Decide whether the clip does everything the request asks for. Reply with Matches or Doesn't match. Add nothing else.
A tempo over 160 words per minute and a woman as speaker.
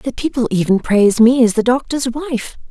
Matches